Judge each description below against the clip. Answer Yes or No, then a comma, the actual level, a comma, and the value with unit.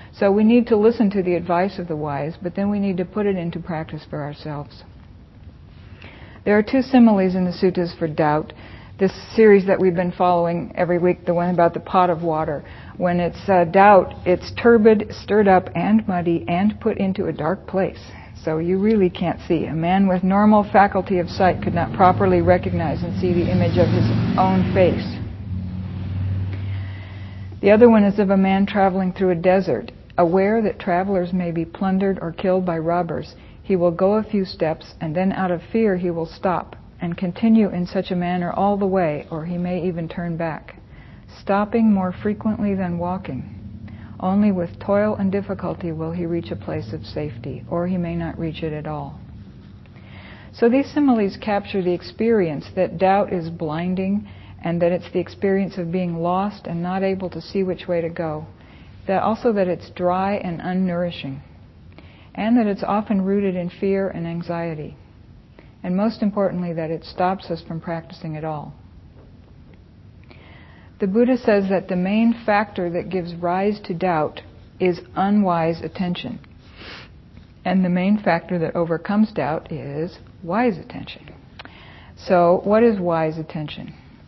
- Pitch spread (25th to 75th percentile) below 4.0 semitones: Yes, average, 3.2 semitones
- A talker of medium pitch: Yes, medium, 180 Hz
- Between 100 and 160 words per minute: No, average, 175 wpm